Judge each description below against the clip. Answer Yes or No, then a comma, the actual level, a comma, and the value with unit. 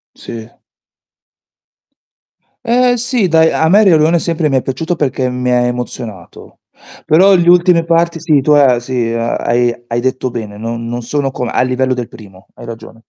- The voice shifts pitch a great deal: Yes, wide, 5.7 semitones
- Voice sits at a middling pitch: No, low, 130 Hz